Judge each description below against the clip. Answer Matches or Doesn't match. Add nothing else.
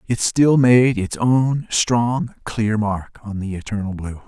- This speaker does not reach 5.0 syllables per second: Matches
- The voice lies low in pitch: Matches